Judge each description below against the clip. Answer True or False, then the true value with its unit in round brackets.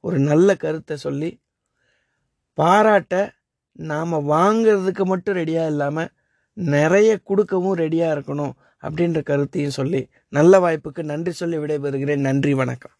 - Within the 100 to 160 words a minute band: True (110 wpm)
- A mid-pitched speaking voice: True (160 Hz)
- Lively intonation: False (4.4 semitones)